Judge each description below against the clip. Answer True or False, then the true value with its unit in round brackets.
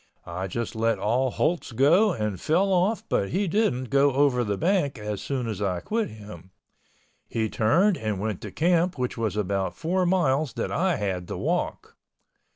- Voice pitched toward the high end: False (125 Hz)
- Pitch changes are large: True (8.6 semitones)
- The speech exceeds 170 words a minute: True (180 wpm)